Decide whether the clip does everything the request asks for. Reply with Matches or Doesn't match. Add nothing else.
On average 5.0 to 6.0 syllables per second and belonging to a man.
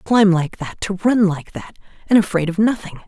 Doesn't match